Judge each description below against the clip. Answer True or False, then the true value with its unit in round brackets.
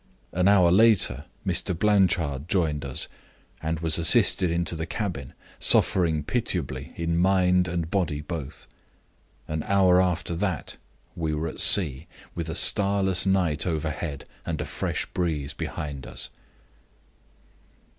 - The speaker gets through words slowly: True (130 wpm)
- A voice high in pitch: False (85 Hz)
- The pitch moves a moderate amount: True (3.2 semitones)